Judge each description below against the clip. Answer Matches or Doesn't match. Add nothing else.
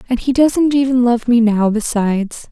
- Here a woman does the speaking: Matches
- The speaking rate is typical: Matches